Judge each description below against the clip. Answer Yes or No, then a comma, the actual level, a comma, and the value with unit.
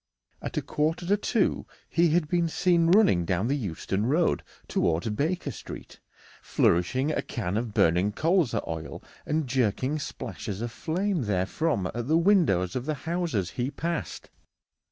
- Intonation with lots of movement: Yes, wide, 8.4 semitones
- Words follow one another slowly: No, average, 155 wpm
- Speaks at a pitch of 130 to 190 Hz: Yes, medium, 140 Hz